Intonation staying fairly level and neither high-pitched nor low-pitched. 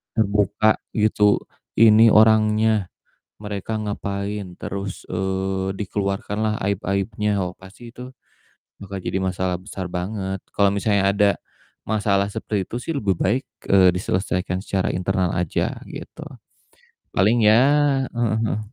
No: narrow, 2.1 semitones; low, 100 Hz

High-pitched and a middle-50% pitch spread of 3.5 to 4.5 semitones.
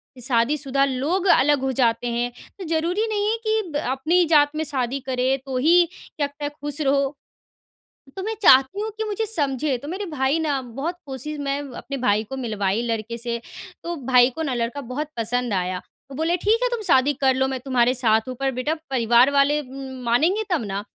Yes: very high, 270 Hz; average, 3.9 semitones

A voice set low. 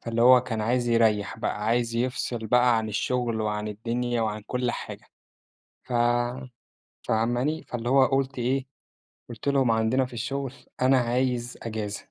Yes: low, 120 Hz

